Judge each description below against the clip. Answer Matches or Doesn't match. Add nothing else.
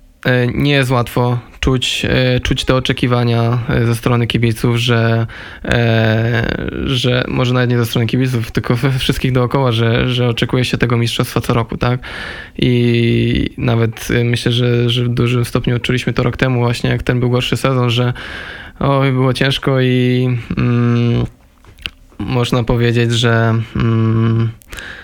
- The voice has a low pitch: Matches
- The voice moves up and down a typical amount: Doesn't match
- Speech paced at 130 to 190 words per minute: Matches